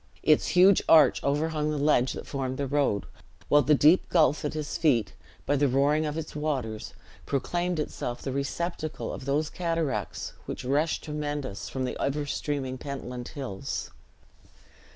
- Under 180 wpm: Yes, average, 155 wpm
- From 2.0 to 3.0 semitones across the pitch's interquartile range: Yes, average, 2.7 semitones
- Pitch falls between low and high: Yes, medium, 145 Hz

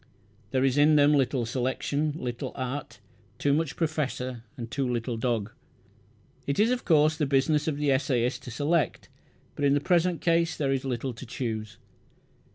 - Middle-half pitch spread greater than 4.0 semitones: No, average, 3.3 semitones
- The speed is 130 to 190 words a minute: Yes, average, 170 wpm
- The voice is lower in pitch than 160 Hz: Yes, medium, 140 Hz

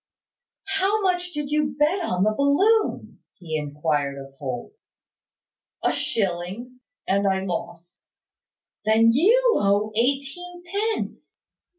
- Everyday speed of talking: No, slow, 110 wpm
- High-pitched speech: Yes, high, 230 Hz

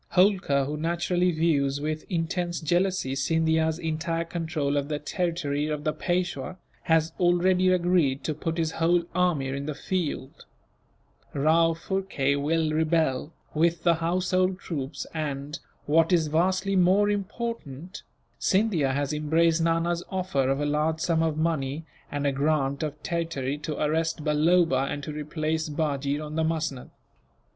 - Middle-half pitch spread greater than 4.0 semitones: No, average, 2.9 semitones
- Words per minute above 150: No, average, 145 wpm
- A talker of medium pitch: Yes, medium, 160 Hz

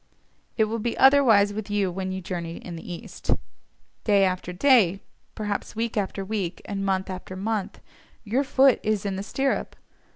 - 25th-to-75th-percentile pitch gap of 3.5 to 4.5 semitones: No, average, 2.8 semitones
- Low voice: No, high, 200 Hz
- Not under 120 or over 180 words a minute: Yes, average, 170 wpm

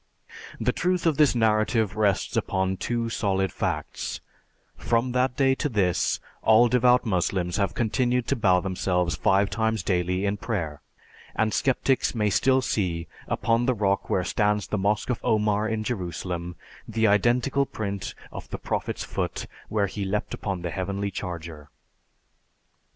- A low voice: Yes, low, 105 Hz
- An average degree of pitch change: Yes, average, 4.0 semitones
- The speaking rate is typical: Yes, average, 150 wpm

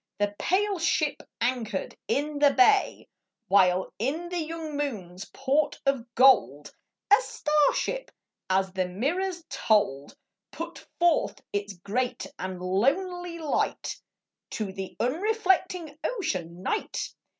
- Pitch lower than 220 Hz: No, very high, 275 Hz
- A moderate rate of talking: No, slow, 125 wpm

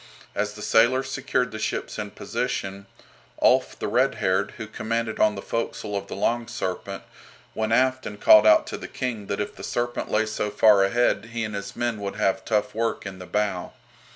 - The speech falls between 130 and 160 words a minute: No, fast, 205 wpm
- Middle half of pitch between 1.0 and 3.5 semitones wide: Yes, narrow, 2.5 semitones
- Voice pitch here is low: Yes, low, 105 Hz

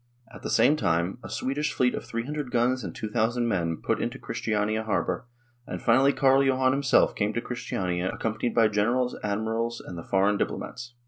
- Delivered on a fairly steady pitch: No, average, 3.6 semitones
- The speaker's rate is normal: Yes, average, 180 wpm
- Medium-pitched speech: No, low, 115 Hz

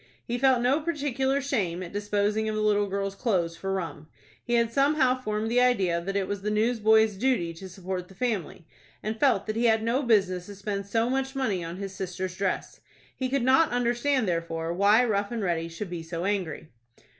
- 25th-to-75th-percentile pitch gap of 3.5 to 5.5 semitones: Yes, average, 4.7 semitones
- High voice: Yes, high, 210 Hz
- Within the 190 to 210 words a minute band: Yes, fast, 205 wpm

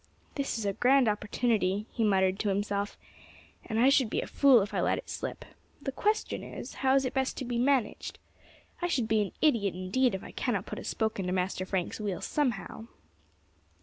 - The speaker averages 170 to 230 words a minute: Yes, fast, 205 wpm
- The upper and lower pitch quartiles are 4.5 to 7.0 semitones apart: Yes, average, 4.8 semitones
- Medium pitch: No, high, 220 Hz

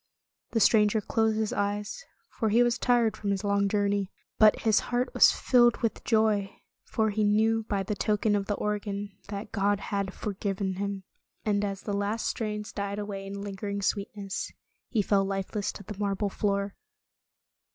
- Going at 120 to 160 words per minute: No, average, 170 wpm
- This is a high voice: Yes, high, 205 Hz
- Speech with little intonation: Yes, narrow, 1.4 semitones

